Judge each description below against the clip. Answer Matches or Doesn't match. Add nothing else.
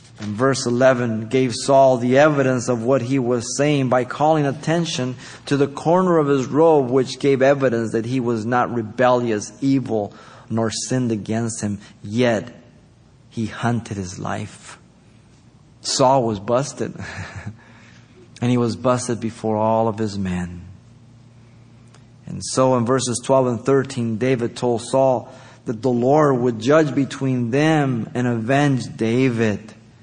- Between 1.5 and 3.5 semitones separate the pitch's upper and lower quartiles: Matches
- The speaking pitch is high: Doesn't match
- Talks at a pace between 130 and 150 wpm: Matches